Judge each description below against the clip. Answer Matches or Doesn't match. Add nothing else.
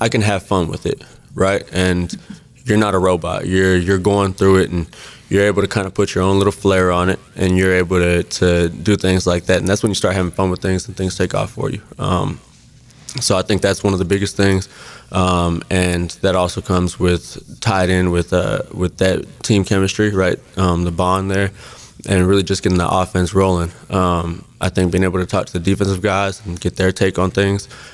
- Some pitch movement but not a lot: Doesn't match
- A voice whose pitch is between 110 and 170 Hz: Doesn't match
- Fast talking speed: Matches